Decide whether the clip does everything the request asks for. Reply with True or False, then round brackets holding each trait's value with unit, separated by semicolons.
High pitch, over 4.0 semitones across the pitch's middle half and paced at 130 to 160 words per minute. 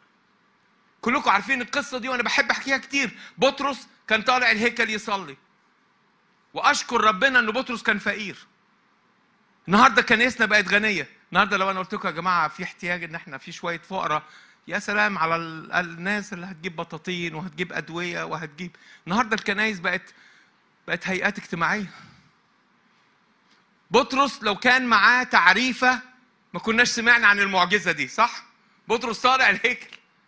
True (210 Hz; 5.1 semitones; 135 wpm)